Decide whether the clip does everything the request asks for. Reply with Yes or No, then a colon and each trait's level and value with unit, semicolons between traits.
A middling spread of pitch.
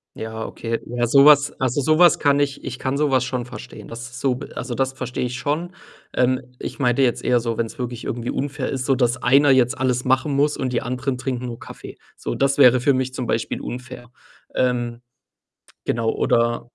No: narrow, 2.0 semitones